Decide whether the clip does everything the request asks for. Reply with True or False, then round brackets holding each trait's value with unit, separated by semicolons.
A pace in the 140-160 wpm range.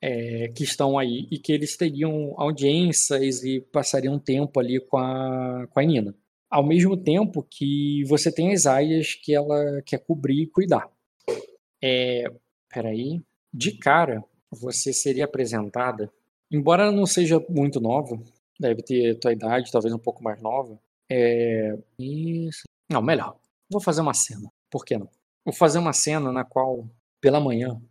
True (155 wpm)